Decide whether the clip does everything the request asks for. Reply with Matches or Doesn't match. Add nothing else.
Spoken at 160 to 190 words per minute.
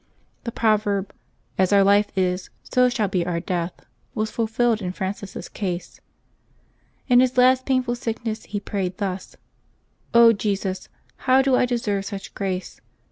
Doesn't match